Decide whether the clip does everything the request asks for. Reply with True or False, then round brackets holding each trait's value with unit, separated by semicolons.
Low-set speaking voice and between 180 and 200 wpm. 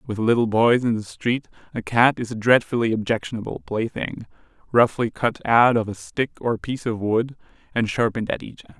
True (115 Hz; 190 wpm)